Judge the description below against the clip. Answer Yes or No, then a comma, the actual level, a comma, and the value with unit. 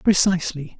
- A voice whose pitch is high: No, medium, 175 Hz